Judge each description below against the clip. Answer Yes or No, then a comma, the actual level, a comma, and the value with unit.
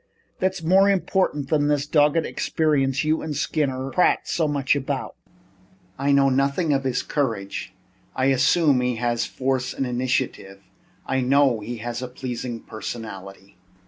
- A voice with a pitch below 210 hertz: Yes, low, 135 Hz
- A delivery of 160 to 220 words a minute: No, average, 150 wpm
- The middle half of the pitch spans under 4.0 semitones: Yes, average, 3.3 semitones